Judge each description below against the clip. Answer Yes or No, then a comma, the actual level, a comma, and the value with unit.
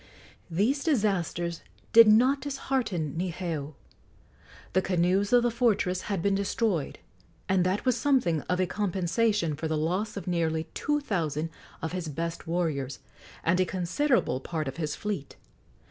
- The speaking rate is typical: Yes, average, 145 wpm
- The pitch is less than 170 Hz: No, medium, 185 Hz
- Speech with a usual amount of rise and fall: Yes, average, 4.7 semitones